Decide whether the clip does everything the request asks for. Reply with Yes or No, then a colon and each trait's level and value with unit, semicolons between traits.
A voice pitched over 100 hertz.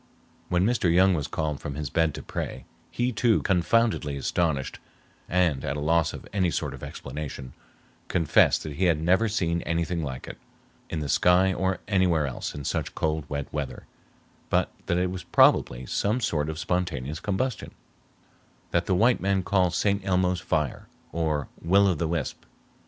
No: very low, 85 Hz